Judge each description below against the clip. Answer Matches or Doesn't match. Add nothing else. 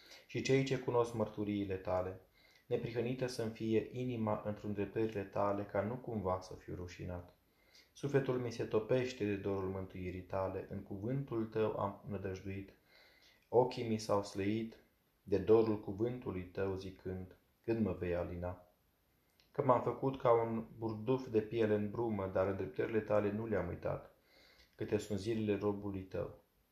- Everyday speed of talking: Matches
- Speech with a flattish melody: Doesn't match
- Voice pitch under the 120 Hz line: Matches